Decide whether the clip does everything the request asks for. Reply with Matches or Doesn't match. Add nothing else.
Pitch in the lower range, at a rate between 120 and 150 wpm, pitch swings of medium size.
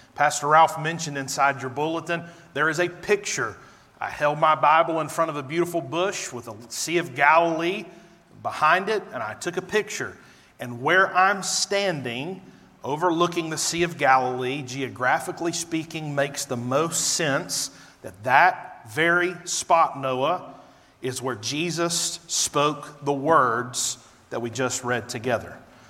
Doesn't match